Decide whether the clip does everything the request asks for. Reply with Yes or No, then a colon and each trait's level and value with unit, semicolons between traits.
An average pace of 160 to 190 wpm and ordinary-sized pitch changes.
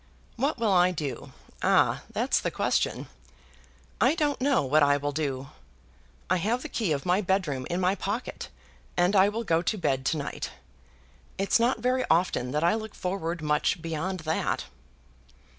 No: average, 170 wpm; wide, 6.0 semitones